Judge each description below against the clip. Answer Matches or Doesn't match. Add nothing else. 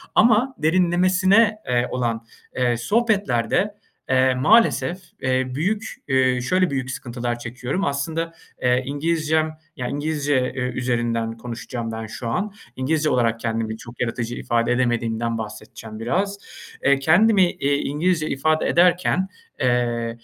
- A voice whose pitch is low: Matches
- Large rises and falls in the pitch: Matches